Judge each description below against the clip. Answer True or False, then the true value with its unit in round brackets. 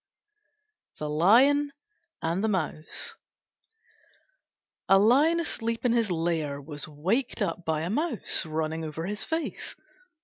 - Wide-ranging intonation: True (7.1 semitones)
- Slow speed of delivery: True (125 wpm)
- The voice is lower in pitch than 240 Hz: True (185 Hz)